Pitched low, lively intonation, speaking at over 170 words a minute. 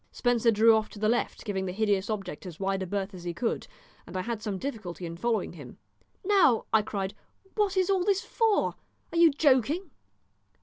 No: high, 220 Hz; wide, 6.6 semitones; fast, 205 wpm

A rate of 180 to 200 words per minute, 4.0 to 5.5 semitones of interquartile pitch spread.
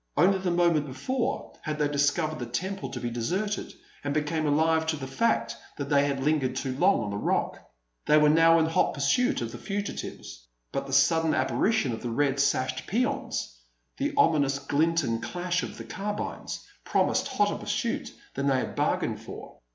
Yes: average, 185 wpm; average, 4.6 semitones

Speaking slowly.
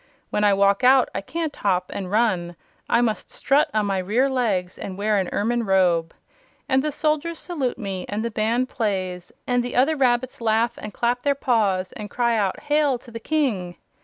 No: average, 195 wpm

